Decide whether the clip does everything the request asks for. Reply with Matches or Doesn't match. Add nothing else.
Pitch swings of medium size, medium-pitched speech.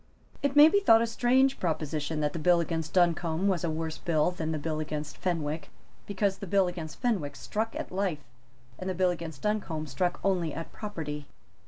Matches